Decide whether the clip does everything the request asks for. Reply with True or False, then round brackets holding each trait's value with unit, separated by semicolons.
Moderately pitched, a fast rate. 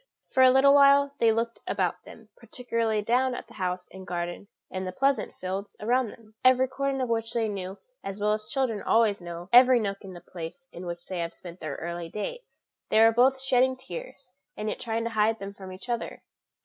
False (220 Hz; 215 wpm)